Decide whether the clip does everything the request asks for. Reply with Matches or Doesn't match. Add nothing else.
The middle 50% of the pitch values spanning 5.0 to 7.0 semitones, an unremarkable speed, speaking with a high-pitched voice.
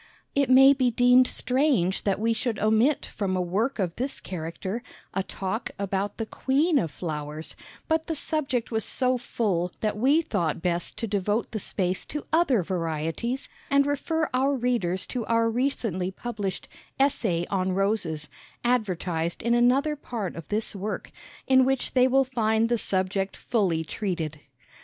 Matches